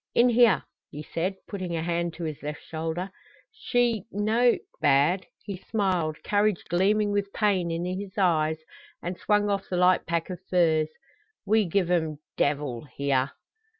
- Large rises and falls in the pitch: No, average, 4.1 semitones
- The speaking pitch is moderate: Yes, medium, 180 Hz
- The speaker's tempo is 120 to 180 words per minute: Yes, average, 155 wpm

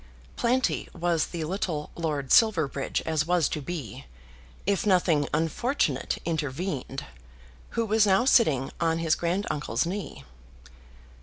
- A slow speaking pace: Yes, slow, 120 wpm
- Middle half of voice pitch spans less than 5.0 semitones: Yes, average, 4.5 semitones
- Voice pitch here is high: No, medium, 165 Hz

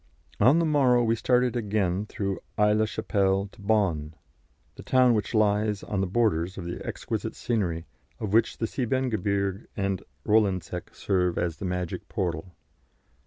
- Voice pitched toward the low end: Yes, low, 100 Hz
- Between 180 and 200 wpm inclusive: No, average, 155 wpm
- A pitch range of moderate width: Yes, average, 3.4 semitones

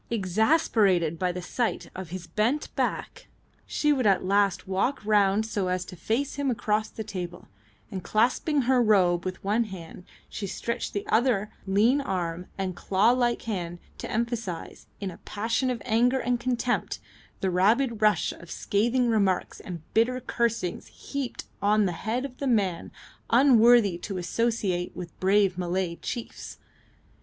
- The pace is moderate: Yes, average, 160 wpm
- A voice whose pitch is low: No, high, 210 Hz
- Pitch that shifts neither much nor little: Yes, average, 4.4 semitones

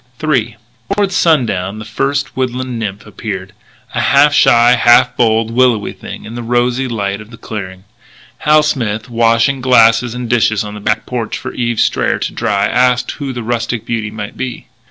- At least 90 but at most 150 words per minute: No, average, 175 wpm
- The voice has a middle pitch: No, low, 120 Hz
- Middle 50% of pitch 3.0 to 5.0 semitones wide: No, narrow, 2.6 semitones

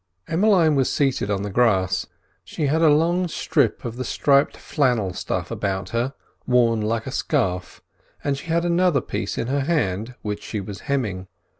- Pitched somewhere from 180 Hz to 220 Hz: No, low, 125 Hz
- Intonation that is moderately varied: No, wide, 6.5 semitones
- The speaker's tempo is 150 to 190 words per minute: Yes, average, 175 wpm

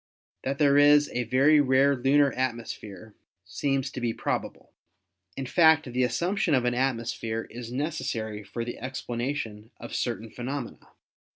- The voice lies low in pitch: Yes, low, 130 Hz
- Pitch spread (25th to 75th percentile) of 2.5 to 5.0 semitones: Yes, average, 3.3 semitones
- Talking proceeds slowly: No, average, 150 wpm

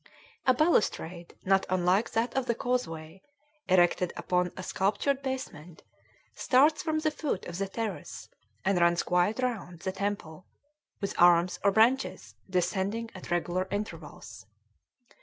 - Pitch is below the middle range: No, high, 190 Hz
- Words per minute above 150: No, slow, 135 wpm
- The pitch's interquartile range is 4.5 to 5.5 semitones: Yes, average, 4.8 semitones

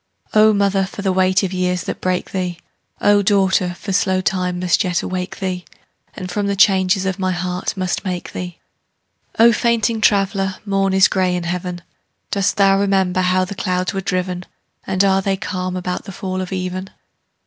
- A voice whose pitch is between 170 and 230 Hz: Yes, medium, 185 Hz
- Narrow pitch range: Yes, narrow, 1.3 semitones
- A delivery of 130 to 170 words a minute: No, average, 185 wpm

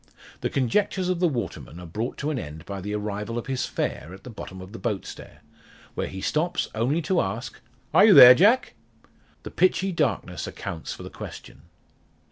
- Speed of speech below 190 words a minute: No, average, 195 wpm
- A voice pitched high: No, low, 120 Hz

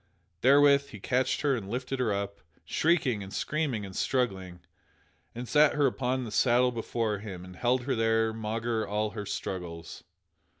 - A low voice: Yes, low, 115 Hz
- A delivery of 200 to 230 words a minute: No, average, 165 wpm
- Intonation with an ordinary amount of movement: Yes, average, 4.1 semitones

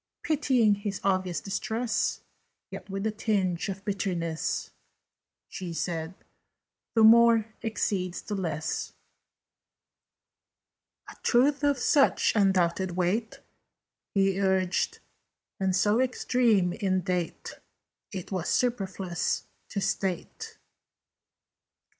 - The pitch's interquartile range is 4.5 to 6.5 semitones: No, average, 3.4 semitones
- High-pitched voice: Yes, high, 195 Hz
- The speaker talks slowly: Yes, slow, 95 wpm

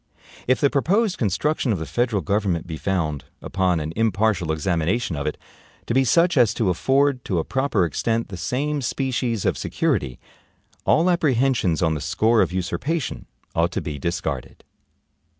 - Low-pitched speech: Yes, low, 110 Hz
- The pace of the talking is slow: No, average, 165 wpm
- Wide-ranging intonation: Yes, wide, 7.6 semitones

